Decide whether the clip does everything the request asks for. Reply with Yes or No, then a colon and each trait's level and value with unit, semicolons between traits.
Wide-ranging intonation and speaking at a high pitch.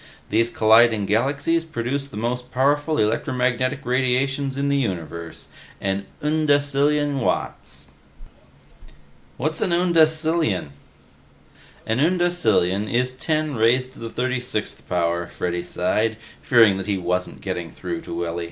No: wide, 5.8 semitones; low, 125 Hz